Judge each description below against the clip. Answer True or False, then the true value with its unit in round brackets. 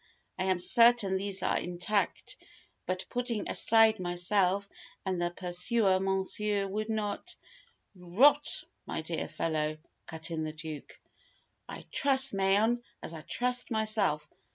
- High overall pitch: True (195 Hz)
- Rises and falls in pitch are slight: False (3.8 semitones)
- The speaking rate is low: True (130 wpm)